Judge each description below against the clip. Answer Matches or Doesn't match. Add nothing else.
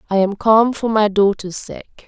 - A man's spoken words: Doesn't match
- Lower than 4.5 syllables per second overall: Matches